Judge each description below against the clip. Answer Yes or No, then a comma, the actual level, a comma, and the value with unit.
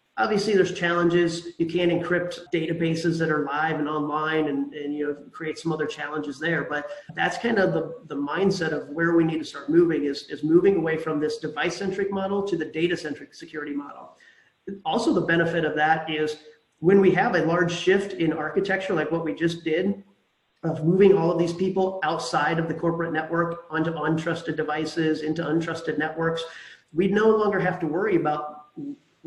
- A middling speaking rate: Yes, average, 190 wpm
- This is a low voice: No, medium, 165 Hz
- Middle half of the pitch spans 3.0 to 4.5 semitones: No, narrow, 2.4 semitones